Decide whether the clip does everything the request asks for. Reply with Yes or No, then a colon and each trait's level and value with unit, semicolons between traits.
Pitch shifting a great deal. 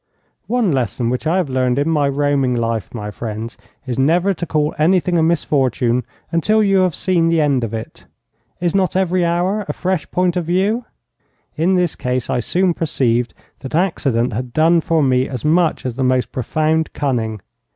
Yes: wide, 5.8 semitones